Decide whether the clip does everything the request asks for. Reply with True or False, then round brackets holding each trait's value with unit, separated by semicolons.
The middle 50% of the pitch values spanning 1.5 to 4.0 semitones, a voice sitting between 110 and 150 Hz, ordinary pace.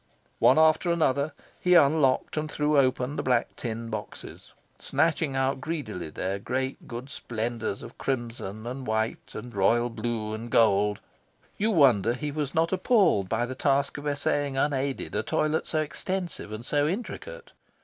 False (5.0 semitones; 135 Hz; 160 wpm)